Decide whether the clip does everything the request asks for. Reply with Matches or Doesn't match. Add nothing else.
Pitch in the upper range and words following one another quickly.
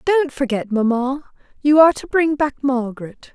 Doesn't match